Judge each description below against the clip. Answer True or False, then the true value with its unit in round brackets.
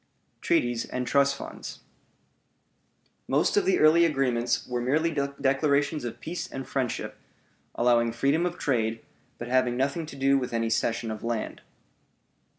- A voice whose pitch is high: False (135 Hz)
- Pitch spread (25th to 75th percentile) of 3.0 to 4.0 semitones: True (3.4 semitones)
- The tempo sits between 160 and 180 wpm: False (145 wpm)